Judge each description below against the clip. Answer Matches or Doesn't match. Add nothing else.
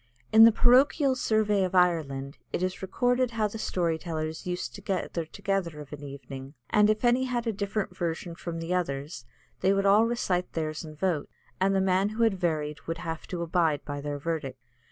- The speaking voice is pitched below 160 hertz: Doesn't match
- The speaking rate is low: Doesn't match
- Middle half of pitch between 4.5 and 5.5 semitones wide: Matches